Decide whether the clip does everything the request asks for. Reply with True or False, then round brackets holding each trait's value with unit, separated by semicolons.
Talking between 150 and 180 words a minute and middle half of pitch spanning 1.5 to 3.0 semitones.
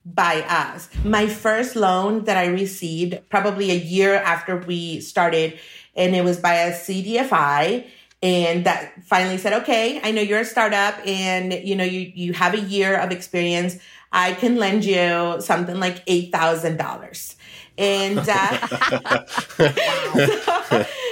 False (140 wpm; 2.7 semitones)